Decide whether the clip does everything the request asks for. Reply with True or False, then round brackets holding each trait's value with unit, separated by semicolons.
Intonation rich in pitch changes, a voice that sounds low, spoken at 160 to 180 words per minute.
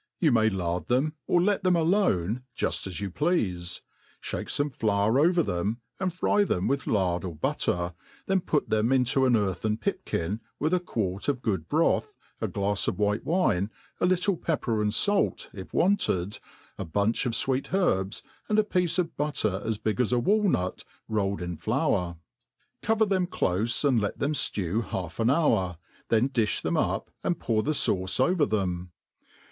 True (8.9 semitones; 115 Hz; 175 wpm)